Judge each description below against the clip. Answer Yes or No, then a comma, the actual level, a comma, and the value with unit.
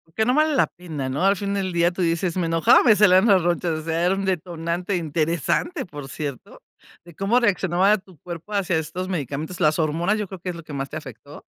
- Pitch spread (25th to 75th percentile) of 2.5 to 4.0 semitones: Yes, average, 3.3 semitones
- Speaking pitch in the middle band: Yes, medium, 175 Hz